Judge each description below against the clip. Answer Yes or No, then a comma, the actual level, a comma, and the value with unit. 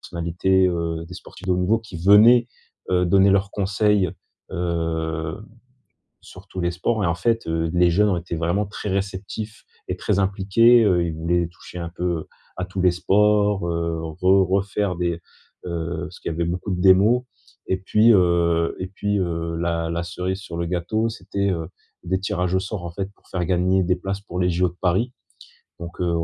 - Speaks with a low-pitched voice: Yes, very low, 90 Hz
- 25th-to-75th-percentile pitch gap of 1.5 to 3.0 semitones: Yes, narrow, 2.5 semitones